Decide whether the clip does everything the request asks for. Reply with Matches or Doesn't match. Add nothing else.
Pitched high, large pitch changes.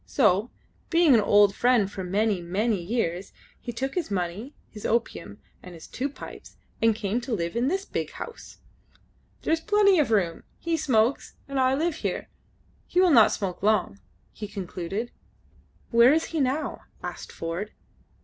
Matches